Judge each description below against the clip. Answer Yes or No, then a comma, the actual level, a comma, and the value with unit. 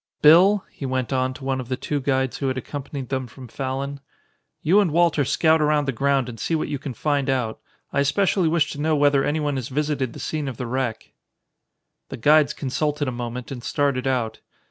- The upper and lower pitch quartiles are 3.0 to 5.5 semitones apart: No, narrow, 2.5 semitones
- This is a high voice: No, medium, 140 Hz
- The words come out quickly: Yes, fast, 210 wpm